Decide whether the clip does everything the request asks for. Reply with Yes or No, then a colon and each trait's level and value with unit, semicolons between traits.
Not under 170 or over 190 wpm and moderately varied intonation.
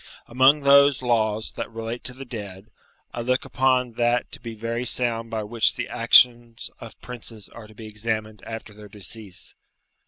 No: average, 175 wpm; narrow, 2.2 semitones